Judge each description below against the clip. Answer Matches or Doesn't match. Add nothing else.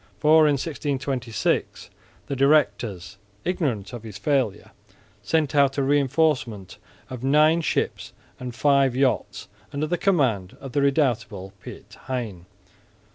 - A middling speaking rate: Doesn't match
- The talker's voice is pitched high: Doesn't match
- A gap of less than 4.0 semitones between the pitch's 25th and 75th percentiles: Doesn't match